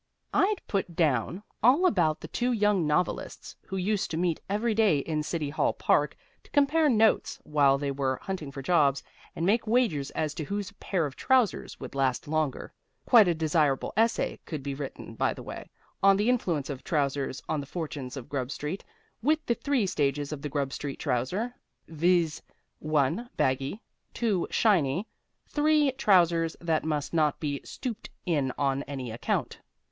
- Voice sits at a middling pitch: Yes, medium, 160 Hz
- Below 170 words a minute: No, average, 175 wpm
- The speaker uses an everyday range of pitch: No, wide, 6.7 semitones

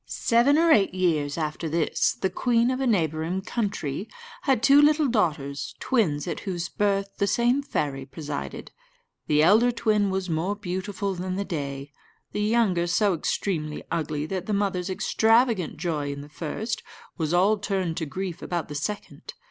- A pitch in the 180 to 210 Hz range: Yes, medium, 185 Hz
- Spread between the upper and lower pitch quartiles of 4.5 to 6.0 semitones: Yes, average, 5.3 semitones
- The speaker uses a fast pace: No, average, 165 wpm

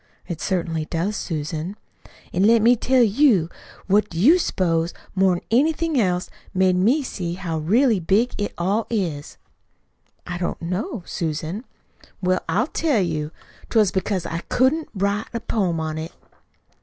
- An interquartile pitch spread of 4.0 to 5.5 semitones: Yes, average, 5.1 semitones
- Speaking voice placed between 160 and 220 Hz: Yes, high, 190 Hz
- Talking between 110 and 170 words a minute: Yes, average, 155 wpm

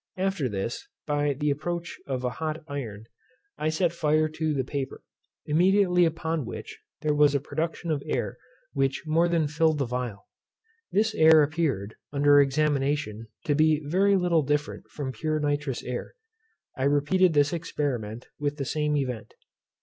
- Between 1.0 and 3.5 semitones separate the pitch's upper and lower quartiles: Yes, average, 2.7 semitones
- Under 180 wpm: Yes, average, 155 wpm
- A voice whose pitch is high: No, medium, 150 Hz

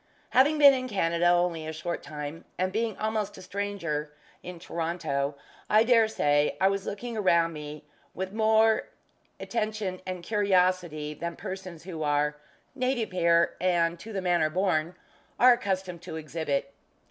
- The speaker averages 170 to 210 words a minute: No, average, 150 wpm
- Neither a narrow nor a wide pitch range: Yes, average, 4.5 semitones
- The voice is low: No, medium, 180 Hz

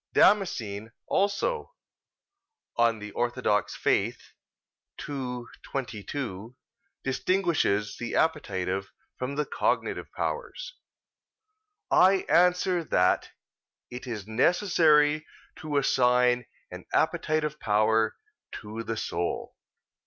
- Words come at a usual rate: No, slow, 85 wpm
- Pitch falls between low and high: No, low, 125 Hz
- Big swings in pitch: Yes, wide, 6.7 semitones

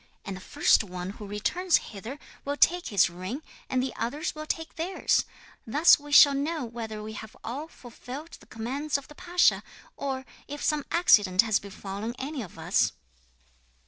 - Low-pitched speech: No, very high, 255 Hz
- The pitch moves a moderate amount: No, wide, 6.3 semitones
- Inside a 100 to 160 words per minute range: No, average, 175 wpm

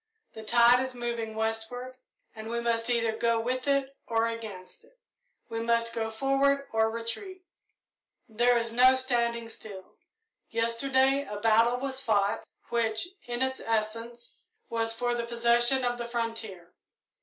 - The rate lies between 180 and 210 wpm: No, average, 145 wpm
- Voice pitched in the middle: No, high, 235 Hz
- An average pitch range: No, narrow, 1.7 semitones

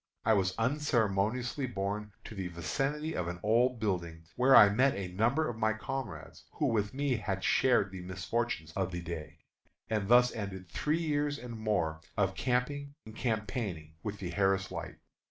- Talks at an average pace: Yes, average, 170 wpm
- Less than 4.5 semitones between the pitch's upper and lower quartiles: No, average, 4.9 semitones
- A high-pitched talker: No, low, 110 Hz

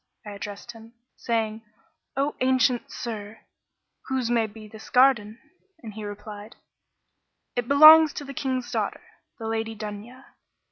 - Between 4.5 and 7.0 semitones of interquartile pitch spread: No, average, 3.2 semitones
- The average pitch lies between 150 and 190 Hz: No, high, 225 Hz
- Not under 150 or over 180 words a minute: No, slow, 135 wpm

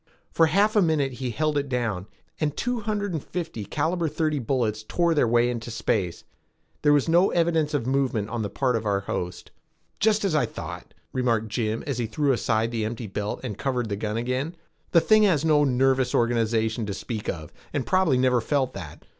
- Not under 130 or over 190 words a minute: No, fast, 205 wpm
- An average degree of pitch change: No, wide, 5.7 semitones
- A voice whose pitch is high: No, low, 130 Hz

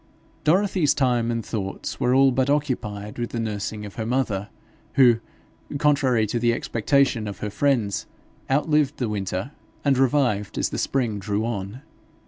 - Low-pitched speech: Yes, low, 120 Hz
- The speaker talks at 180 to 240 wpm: No, average, 155 wpm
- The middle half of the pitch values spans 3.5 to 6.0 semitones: Yes, average, 4.5 semitones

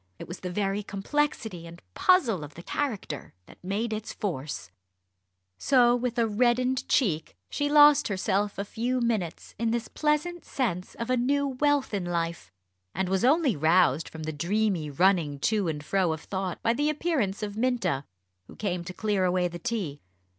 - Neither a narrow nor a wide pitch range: No, wide, 6.1 semitones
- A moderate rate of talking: Yes, average, 175 wpm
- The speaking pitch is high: Yes, high, 205 Hz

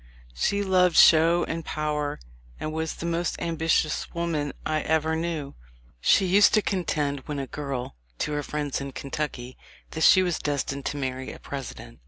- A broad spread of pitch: No, average, 2.9 semitones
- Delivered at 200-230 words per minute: No, average, 175 wpm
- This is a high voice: No, medium, 155 Hz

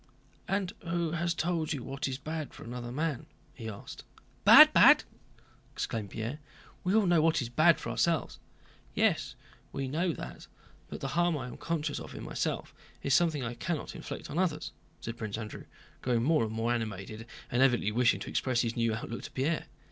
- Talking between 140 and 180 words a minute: No, average, 190 wpm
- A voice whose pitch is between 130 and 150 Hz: Yes, low, 135 Hz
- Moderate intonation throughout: No, wide, 5.7 semitones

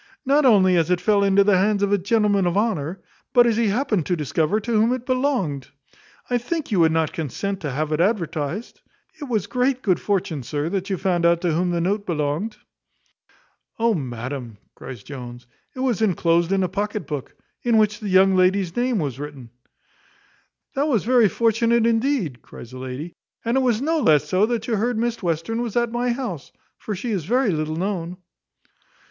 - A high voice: Yes, high, 195 Hz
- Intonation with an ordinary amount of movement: No, wide, 6.1 semitones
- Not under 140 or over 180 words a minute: No, average, 200 wpm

